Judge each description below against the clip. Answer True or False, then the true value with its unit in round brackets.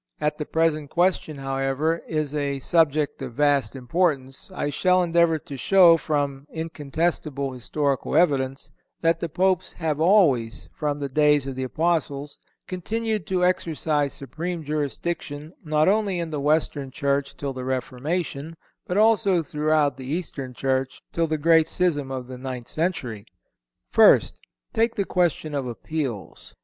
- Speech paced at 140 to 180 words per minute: True (145 wpm)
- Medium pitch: True (150 Hz)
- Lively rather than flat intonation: False (3.6 semitones)